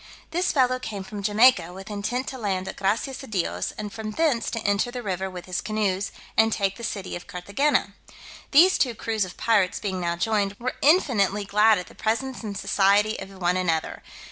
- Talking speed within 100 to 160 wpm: No, average, 200 wpm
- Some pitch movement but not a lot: Yes, average, 3.6 semitones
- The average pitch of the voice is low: No, high, 210 Hz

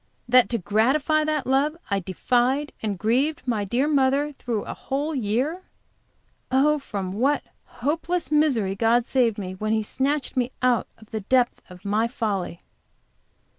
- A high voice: Yes, very high, 250 Hz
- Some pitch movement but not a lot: Yes, average, 5.0 semitones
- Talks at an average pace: Yes, average, 155 wpm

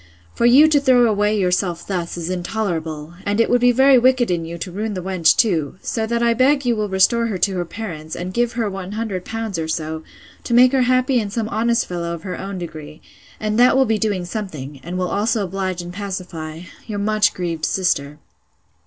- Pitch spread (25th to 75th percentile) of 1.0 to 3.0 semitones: No, average, 4.9 semitones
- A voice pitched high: Yes, high, 200 Hz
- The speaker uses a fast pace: Yes, fast, 215 wpm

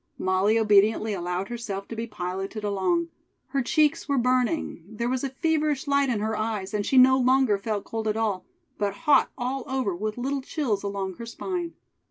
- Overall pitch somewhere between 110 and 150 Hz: No, high, 225 Hz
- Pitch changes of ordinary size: Yes, average, 4.7 semitones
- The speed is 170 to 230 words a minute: Yes, average, 190 wpm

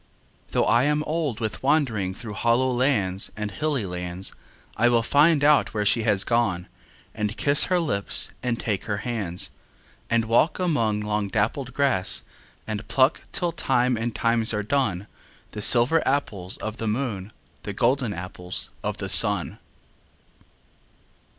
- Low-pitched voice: Yes, low, 115 Hz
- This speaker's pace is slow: No, average, 150 wpm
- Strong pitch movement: No, average, 4.6 semitones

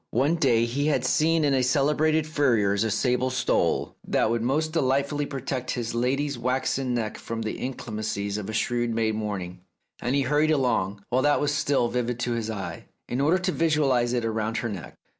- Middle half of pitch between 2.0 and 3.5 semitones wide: No, average, 4.0 semitones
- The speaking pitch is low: Yes, low, 125 Hz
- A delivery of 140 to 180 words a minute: No, average, 195 wpm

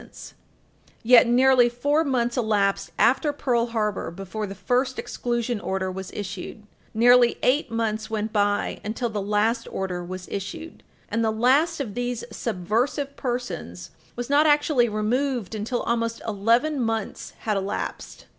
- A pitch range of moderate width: Yes, average, 3.3 semitones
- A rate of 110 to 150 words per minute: Yes, average, 145 wpm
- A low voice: No, high, 230 Hz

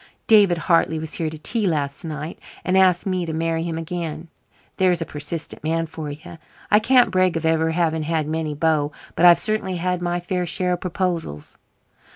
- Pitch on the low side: No, medium, 165 Hz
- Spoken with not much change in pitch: Yes, narrow, 2.2 semitones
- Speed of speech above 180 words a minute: Yes, average, 190 wpm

